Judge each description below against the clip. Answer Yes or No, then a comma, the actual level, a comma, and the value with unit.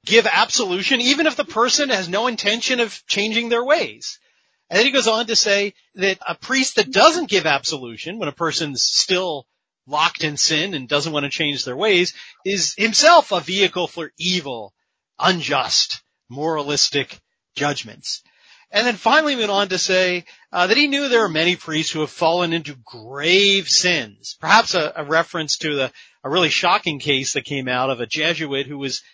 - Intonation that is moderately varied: No, wide, 6.8 semitones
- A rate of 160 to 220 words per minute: Yes, average, 185 wpm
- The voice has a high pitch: No, medium, 180 Hz